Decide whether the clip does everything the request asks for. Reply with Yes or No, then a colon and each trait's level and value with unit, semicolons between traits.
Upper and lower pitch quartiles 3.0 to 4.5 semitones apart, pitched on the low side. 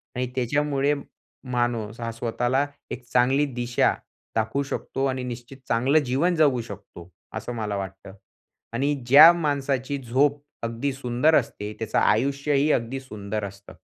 Yes: average, 3.4 semitones; low, 125 Hz